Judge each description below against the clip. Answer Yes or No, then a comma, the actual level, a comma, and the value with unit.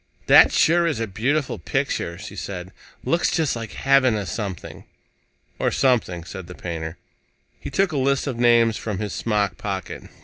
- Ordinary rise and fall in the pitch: No, wide, 6.2 semitones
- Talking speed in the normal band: Yes, average, 170 wpm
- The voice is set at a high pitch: No, low, 115 Hz